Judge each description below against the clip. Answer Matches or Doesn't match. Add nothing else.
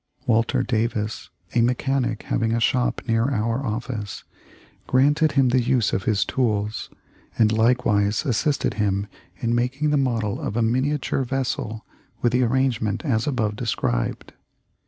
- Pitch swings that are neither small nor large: Matches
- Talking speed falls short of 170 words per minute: Matches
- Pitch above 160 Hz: Doesn't match